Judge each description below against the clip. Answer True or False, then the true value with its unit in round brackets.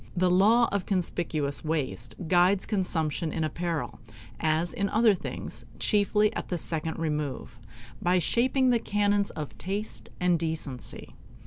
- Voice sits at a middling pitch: True (175 Hz)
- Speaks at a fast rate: False (135 wpm)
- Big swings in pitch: False (4.4 semitones)